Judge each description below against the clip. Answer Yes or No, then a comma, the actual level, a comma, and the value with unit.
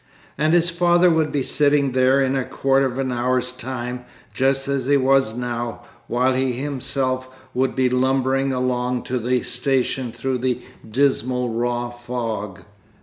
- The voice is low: Yes, low, 130 Hz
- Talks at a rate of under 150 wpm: No, average, 155 wpm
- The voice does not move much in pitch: Yes, narrow, 1.6 semitones